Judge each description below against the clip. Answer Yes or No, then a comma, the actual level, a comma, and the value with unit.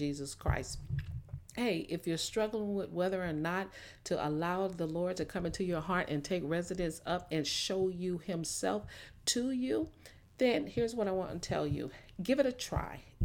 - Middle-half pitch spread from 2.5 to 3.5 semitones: Yes, average, 2.9 semitones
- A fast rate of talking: No, average, 185 wpm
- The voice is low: No, medium, 180 Hz